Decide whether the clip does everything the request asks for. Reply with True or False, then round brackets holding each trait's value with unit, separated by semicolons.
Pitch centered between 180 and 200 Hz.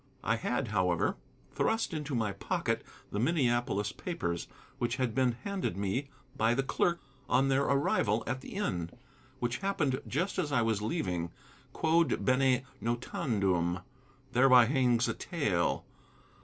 False (125 Hz)